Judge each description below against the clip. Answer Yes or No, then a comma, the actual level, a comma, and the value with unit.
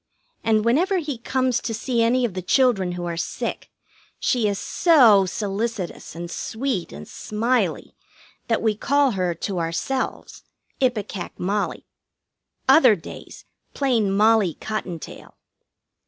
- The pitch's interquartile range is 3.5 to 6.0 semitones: Yes, average, 5.0 semitones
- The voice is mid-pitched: No, high, 220 Hz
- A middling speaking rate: No, slow, 125 wpm